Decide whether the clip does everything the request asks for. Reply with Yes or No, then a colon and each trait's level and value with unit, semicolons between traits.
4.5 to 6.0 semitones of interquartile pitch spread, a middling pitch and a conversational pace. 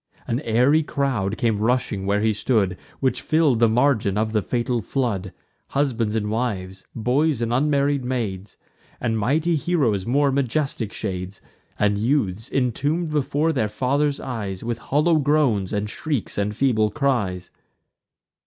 No: average, 5.0 semitones; low, 120 Hz; average, 145 wpm